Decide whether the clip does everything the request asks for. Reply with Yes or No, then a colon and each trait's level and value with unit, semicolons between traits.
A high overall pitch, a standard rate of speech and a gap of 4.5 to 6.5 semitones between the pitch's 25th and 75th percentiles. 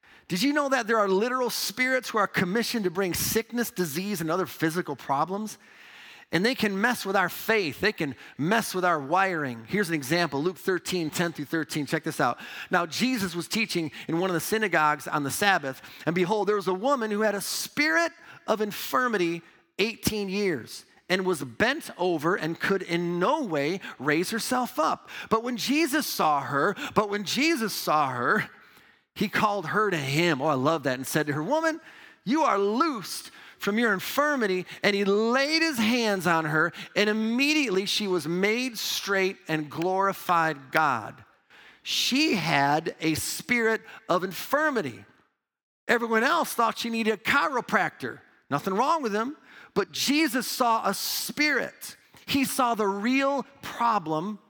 Yes: high, 200 Hz; average, 170 wpm; wide, 5.4 semitones